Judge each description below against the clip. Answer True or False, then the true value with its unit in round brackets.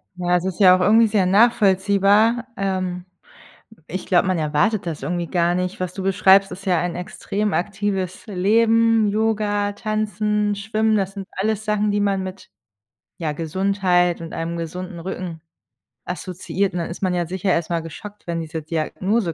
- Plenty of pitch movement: False (2.8 semitones)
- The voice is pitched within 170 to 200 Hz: True (190 Hz)